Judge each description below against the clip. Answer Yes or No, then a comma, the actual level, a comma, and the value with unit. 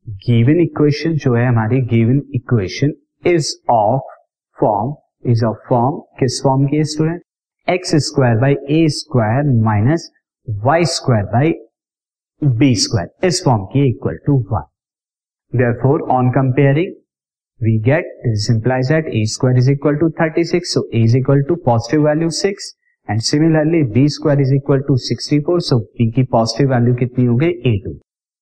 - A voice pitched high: No, low, 135 Hz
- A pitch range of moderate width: Yes, average, 4.3 semitones